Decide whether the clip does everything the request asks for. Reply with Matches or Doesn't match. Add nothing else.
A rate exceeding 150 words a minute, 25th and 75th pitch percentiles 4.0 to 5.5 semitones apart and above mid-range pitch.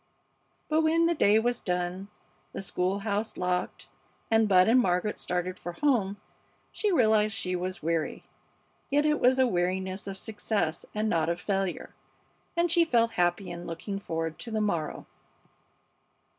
Matches